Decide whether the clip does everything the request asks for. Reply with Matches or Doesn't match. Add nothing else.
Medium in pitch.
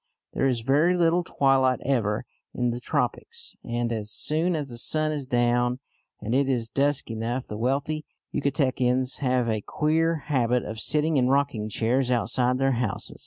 Doesn't match